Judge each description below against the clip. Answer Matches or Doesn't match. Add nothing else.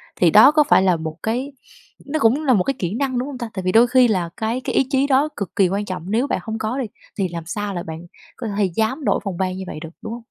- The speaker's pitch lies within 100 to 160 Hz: Doesn't match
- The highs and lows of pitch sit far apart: Matches